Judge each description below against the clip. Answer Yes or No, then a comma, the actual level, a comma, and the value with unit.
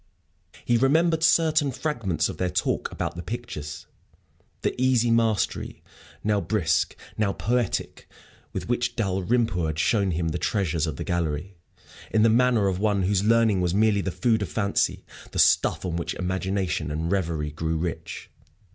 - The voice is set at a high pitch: No, low, 100 Hz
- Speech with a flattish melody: No, average, 5.1 semitones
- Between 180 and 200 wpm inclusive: No, average, 160 wpm